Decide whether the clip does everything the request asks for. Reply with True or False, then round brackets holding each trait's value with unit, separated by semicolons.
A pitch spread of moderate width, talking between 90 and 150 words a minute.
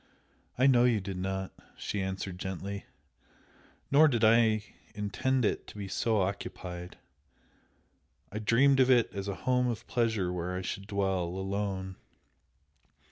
True (3.7 semitones; 140 wpm)